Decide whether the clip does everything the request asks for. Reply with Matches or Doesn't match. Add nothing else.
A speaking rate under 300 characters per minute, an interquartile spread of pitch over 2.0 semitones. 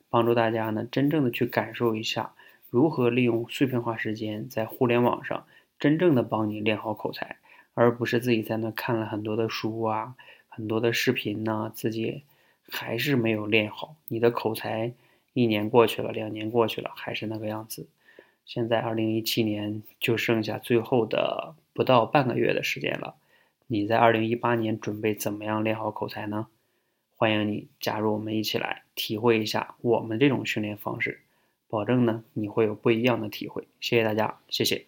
Doesn't match